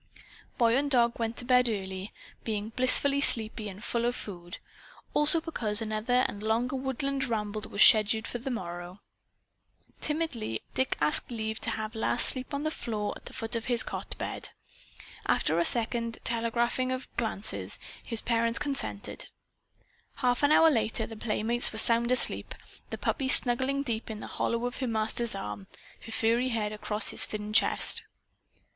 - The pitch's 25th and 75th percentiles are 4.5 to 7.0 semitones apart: No, average, 2.8 semitones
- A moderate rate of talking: Yes, average, 160 wpm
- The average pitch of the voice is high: Yes, high, 230 Hz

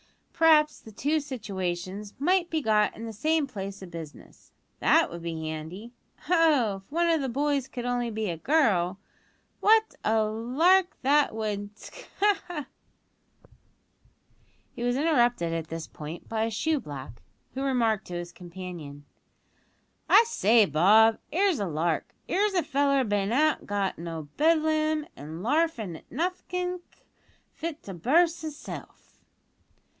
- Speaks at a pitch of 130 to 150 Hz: No, high, 230 Hz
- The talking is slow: No, average, 150 wpm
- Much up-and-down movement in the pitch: Yes, wide, 8.7 semitones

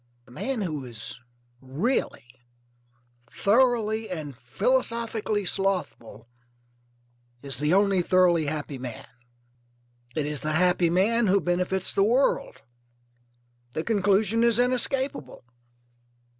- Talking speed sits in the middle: No, slow, 100 wpm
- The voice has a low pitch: No, medium, 185 Hz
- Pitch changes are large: Yes, wide, 6.9 semitones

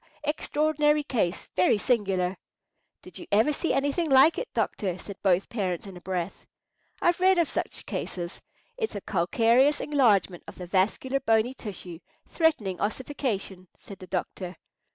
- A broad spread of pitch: Yes, wide, 7.6 semitones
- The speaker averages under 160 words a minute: Yes, average, 150 wpm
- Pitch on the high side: Yes, high, 215 Hz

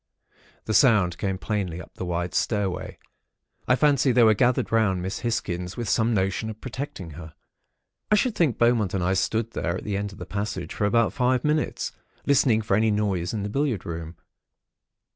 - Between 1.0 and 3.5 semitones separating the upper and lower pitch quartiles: No, average, 4.2 semitones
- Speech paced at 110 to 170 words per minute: No, average, 195 wpm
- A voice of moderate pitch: No, low, 105 Hz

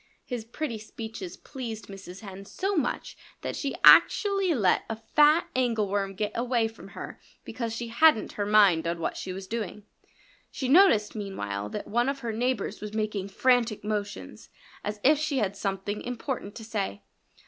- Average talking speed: Yes, average, 170 wpm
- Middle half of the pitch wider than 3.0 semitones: Yes, average, 3.8 semitones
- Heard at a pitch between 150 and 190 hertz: No, high, 220 Hz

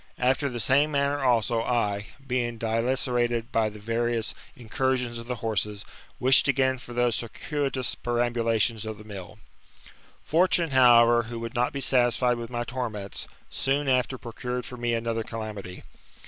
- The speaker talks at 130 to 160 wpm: Yes, average, 155 wpm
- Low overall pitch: Yes, low, 120 Hz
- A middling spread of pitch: No, narrow, 2.1 semitones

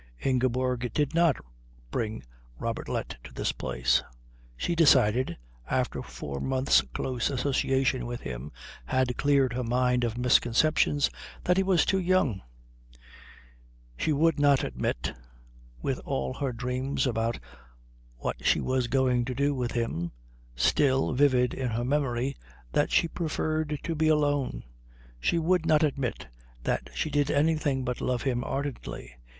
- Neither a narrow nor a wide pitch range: Yes, average, 3.3 semitones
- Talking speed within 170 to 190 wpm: No, average, 140 wpm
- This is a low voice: Yes, low, 130 Hz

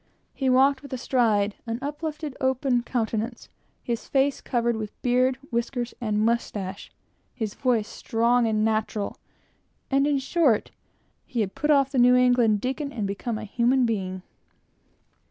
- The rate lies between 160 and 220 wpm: No, average, 150 wpm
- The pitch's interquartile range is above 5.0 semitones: No, average, 3.3 semitones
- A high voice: Yes, high, 240 Hz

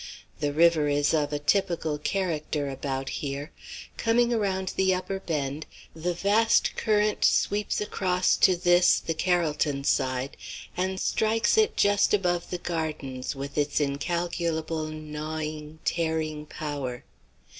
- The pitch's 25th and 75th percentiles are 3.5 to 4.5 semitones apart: Yes, average, 4.1 semitones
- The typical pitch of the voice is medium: Yes, medium, 160 Hz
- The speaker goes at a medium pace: No, slow, 125 wpm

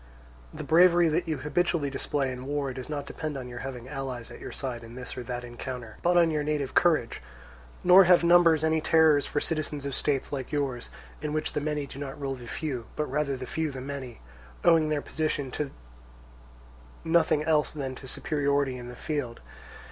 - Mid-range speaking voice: Yes, medium, 145 Hz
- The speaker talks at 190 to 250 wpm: Yes, average, 200 wpm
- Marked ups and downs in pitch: No, average, 3.1 semitones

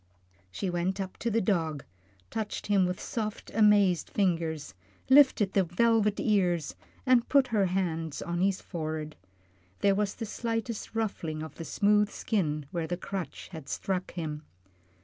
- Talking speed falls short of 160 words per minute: Yes, average, 150 wpm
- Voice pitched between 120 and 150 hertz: No, high, 190 Hz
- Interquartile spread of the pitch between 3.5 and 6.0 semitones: Yes, average, 4.3 semitones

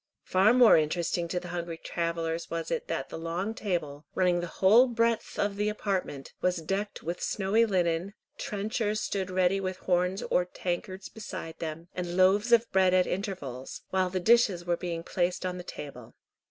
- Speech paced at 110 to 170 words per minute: No, average, 180 wpm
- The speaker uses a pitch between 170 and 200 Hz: Yes, medium, 185 Hz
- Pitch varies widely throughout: No, average, 2.9 semitones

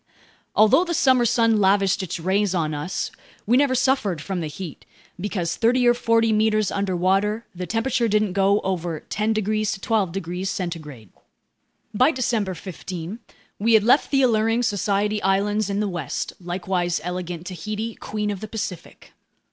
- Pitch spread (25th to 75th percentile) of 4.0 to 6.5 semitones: No, average, 3.6 semitones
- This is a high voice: Yes, high, 205 Hz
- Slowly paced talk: No, average, 160 wpm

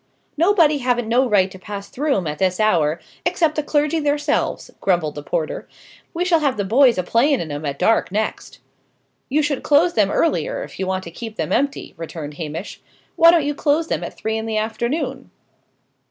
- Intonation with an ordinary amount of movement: No, wide, 8.0 semitones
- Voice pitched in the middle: No, high, 230 Hz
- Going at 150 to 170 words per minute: No, average, 200 wpm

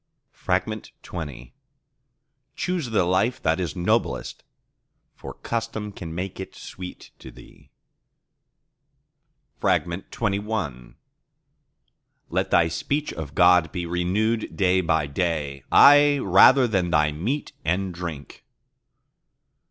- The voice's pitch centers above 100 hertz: No, very low, 90 Hz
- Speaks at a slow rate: Yes, slow, 100 wpm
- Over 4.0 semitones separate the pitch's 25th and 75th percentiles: Yes, average, 4.9 semitones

